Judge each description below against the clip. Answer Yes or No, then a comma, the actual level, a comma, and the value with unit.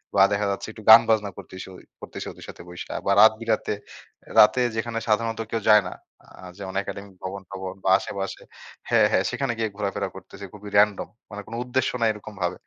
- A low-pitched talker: Yes, low, 105 Hz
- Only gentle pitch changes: Yes, narrow, 2.3 semitones